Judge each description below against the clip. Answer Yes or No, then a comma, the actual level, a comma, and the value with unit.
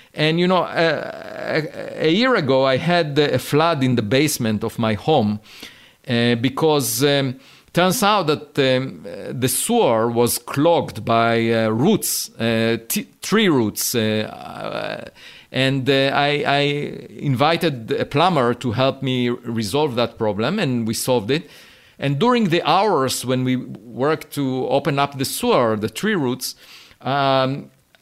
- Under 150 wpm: Yes, slow, 135 wpm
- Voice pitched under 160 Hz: Yes, low, 135 Hz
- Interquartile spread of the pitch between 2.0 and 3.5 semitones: No, average, 4.3 semitones